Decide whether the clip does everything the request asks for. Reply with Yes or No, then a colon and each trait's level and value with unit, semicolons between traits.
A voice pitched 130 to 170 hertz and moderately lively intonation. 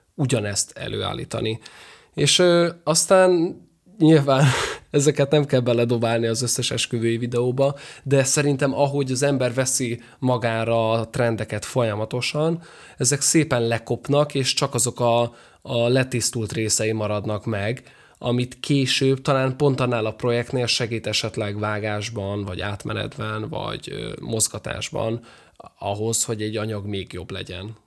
No: low, 120 Hz; average, 3.9 semitones